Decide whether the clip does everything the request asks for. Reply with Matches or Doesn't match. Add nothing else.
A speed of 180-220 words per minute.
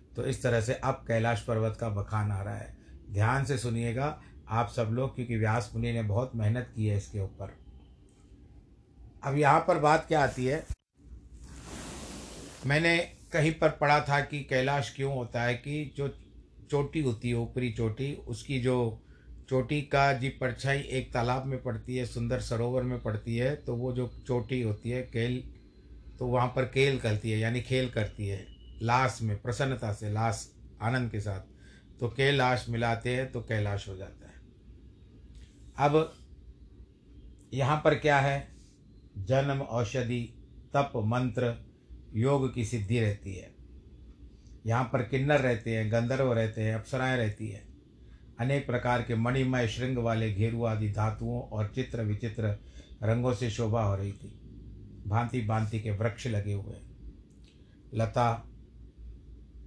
Doesn't match